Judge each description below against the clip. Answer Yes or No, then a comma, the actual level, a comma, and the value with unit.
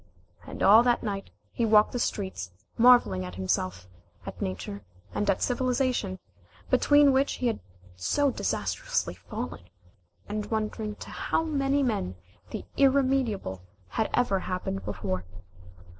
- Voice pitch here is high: Yes, high, 215 Hz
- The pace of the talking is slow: Yes, slow, 130 wpm